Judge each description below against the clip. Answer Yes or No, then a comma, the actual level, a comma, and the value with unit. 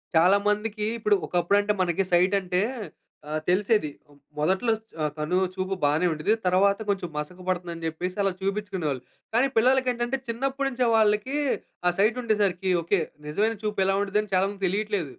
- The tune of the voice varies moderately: Yes, average, 3.2 semitones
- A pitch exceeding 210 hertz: No, high, 195 Hz